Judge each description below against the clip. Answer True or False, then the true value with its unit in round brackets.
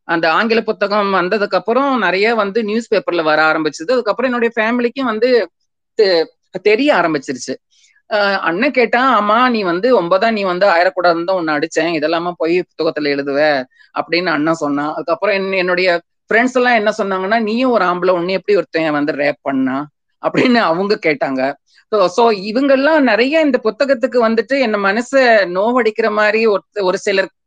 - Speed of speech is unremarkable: False (140 wpm)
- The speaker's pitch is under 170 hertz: False (205 Hz)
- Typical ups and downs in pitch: False (6.0 semitones)